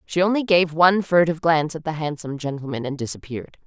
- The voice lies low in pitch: No, medium, 160 Hz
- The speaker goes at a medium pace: Yes, average, 195 wpm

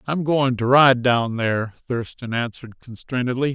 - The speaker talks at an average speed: Yes, average, 150 wpm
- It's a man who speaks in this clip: Yes, male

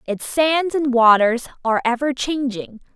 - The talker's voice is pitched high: Yes, very high, 260 Hz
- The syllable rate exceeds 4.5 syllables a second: No, 4.4 syllables/s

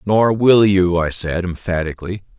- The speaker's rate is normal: Yes, average, 150 wpm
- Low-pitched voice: Yes, very low, 95 Hz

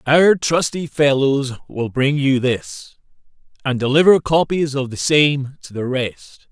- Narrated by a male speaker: Yes, male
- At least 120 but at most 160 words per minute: Yes, average, 145 wpm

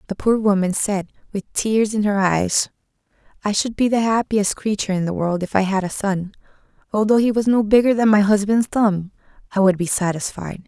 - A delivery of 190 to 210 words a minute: Yes, average, 200 wpm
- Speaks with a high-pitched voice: Yes, high, 205 Hz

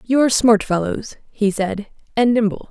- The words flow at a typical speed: Yes, average, 175 wpm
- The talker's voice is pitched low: No, high, 220 Hz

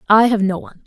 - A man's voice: No, female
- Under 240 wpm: No, fast, 275 wpm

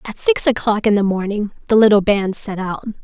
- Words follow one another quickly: Yes, fast, 220 wpm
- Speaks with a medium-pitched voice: No, high, 210 Hz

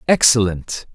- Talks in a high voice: No, low, 110 Hz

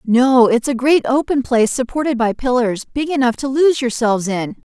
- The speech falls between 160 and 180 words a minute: No, average, 190 wpm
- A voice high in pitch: Yes, very high, 250 Hz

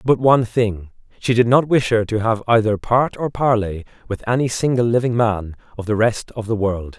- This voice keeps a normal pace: No, fast, 215 wpm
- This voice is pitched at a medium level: No, low, 115 Hz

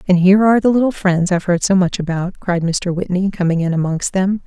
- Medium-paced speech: No, fast, 240 wpm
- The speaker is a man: No, female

